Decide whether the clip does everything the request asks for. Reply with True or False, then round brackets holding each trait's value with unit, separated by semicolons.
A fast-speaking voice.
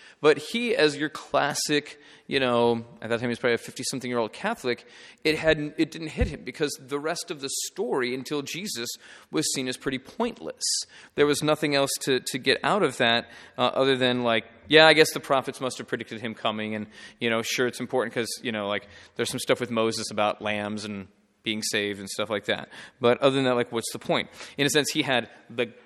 True (225 wpm)